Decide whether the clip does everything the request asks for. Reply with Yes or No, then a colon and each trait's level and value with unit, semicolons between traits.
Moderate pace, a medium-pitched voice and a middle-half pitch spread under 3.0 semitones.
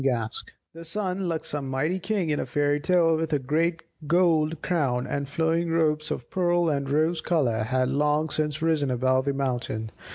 No: average, 185 wpm; medium, 150 Hz; average, 3.6 semitones